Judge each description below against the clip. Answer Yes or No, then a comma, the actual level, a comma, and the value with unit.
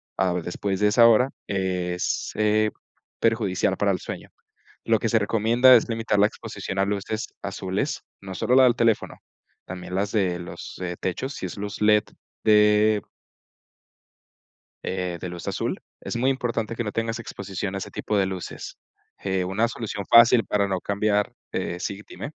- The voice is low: Yes, low, 105 Hz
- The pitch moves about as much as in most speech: Yes, average, 3.0 semitones